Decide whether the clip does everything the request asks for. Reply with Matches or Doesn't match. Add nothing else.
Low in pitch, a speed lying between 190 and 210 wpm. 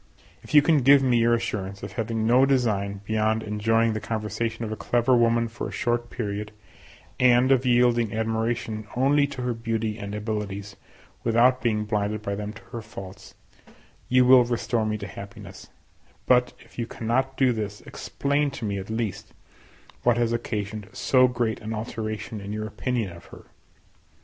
Doesn't match